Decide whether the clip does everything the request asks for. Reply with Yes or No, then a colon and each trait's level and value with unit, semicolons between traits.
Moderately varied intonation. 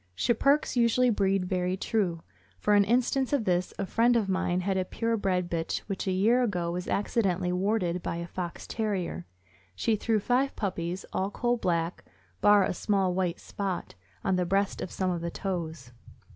Yes: average, 3.6 semitones